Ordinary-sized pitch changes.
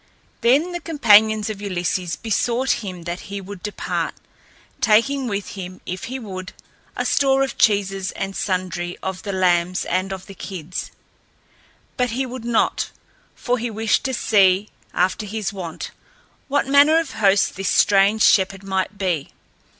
Yes: average, 4.0 semitones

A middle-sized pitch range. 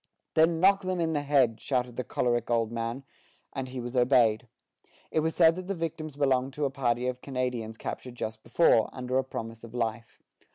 Yes: average, 3.8 semitones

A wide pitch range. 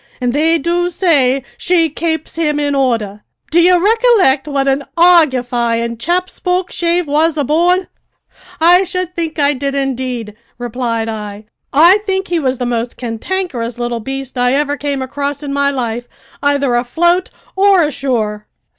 Yes: wide, 5.8 semitones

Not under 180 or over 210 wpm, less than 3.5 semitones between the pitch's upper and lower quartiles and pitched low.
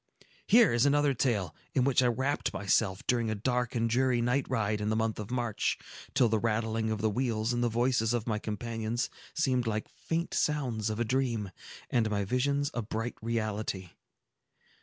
Yes: average, 185 wpm; narrow, 2.6 semitones; low, 115 Hz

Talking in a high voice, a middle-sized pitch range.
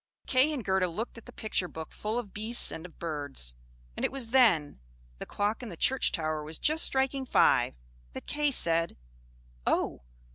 No: high, 210 Hz; wide, 7.7 semitones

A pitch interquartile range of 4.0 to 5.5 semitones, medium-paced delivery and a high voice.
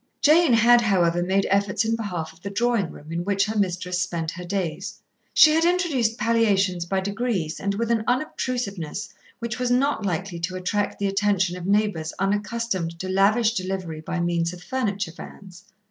Yes: average, 4.3 semitones; average, 175 wpm; high, 200 Hz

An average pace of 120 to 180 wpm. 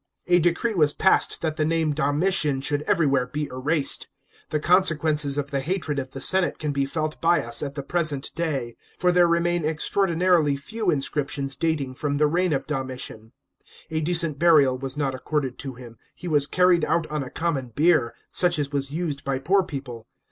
No: average, 195 wpm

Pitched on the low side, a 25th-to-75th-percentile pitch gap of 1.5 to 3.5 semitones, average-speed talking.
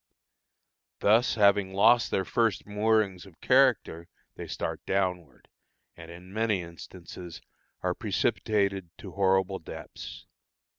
No: very low, 95 Hz; average, 3.1 semitones; slow, 110 wpm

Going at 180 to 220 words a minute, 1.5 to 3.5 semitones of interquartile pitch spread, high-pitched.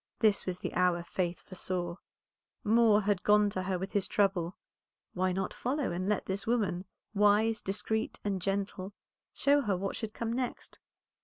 No: average, 165 wpm; narrow, 2.5 semitones; high, 200 Hz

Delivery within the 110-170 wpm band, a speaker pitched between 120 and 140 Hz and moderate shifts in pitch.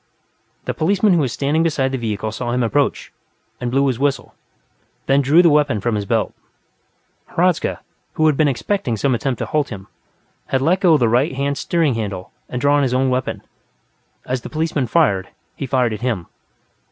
No: average, 190 wpm; low, 135 Hz; average, 4.3 semitones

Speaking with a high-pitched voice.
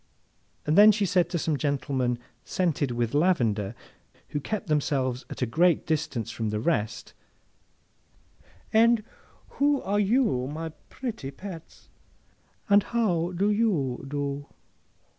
No: medium, 155 Hz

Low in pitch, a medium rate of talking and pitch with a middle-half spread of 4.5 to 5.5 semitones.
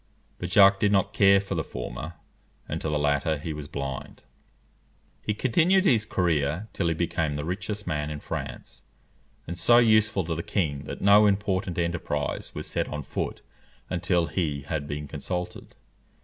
Yes: very low, 85 Hz; average, 170 wpm; average, 5.1 semitones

